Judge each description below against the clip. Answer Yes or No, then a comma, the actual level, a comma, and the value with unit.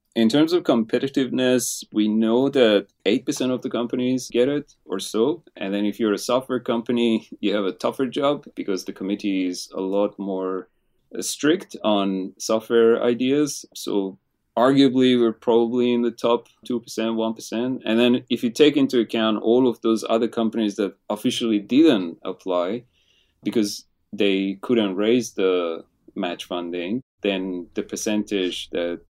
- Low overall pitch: Yes, low, 115 Hz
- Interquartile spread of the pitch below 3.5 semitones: No, average, 3.8 semitones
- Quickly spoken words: No, average, 150 wpm